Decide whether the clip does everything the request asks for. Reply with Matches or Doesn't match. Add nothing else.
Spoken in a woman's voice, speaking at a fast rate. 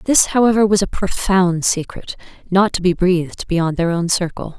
Doesn't match